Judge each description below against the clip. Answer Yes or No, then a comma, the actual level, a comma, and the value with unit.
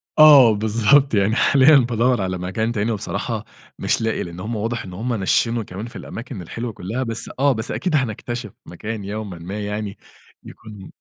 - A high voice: No, low, 110 Hz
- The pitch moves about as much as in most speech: Yes, average, 3.0 semitones